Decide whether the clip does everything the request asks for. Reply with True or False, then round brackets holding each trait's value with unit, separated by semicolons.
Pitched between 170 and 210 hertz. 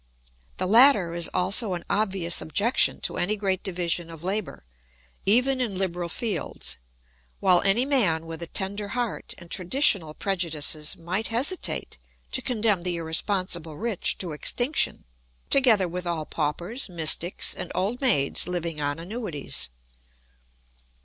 True (185 Hz)